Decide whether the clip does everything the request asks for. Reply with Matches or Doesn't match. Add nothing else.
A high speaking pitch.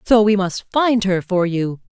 Matches